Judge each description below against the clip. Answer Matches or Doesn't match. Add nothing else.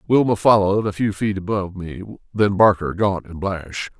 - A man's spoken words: Matches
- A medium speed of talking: Matches